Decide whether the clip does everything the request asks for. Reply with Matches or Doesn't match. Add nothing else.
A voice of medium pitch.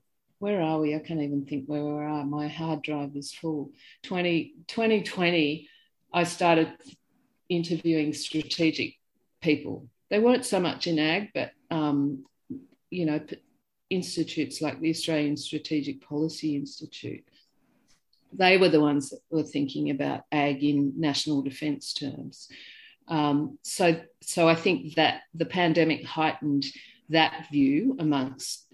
Matches